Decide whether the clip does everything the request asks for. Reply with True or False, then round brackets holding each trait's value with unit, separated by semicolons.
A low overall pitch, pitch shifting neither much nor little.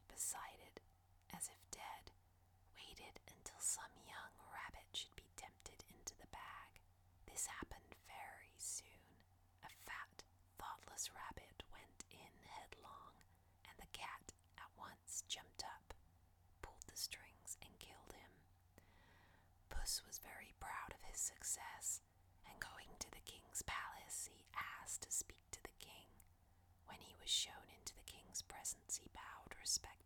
False (90 Hz; 0.7 semitones)